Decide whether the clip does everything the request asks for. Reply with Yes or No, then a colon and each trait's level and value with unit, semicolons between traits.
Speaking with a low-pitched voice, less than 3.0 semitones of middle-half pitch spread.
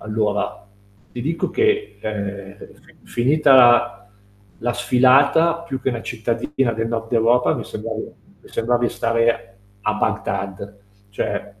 No: low, 115 Hz; average, 3.3 semitones